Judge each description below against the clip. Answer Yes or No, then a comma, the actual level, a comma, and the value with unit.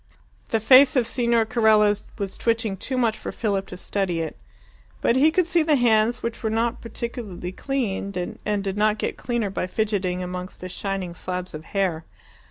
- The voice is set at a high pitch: Yes, high, 215 Hz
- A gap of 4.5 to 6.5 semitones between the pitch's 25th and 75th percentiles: No, average, 3.8 semitones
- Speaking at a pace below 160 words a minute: No, average, 180 wpm